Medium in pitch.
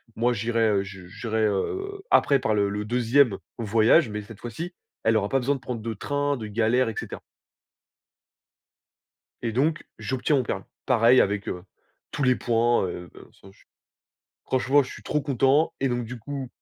No: low, 120 Hz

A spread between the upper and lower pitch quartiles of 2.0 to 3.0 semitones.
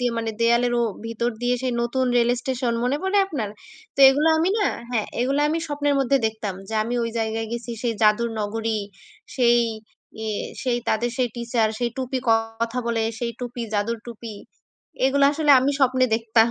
Yes: narrow, 2.5 semitones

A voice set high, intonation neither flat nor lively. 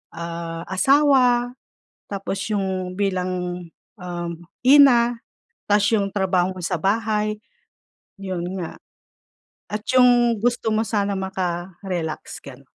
Yes: high, 195 Hz; average, 4.0 semitones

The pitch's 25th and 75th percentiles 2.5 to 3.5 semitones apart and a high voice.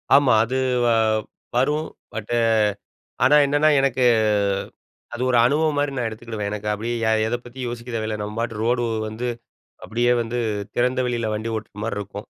No: average, 2.8 semitones; low, 120 Hz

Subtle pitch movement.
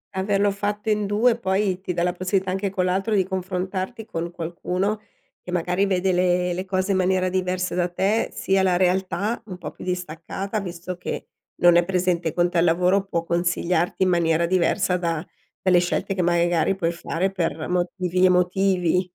Yes: narrow, 1.5 semitones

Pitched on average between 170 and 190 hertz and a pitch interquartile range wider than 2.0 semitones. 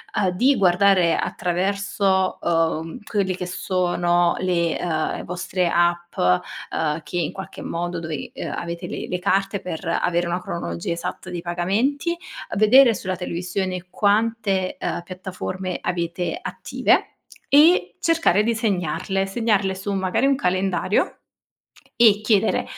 Yes: medium, 185 Hz; narrow, 2.6 semitones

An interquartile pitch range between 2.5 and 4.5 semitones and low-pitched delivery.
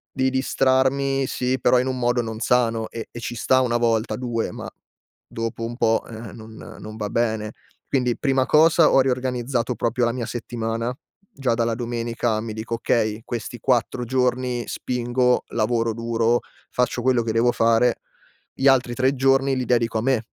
No: narrow, 2.0 semitones; low, 120 Hz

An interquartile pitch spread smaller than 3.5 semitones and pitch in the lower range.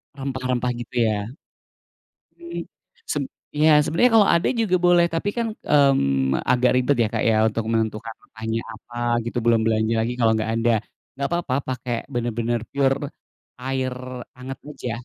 No: average, 3.9 semitones; low, 125 Hz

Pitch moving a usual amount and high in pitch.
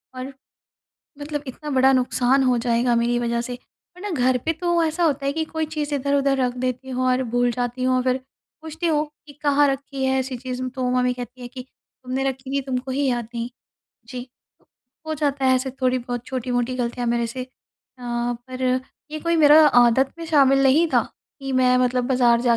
No: narrow, 2.3 semitones; very high, 255 Hz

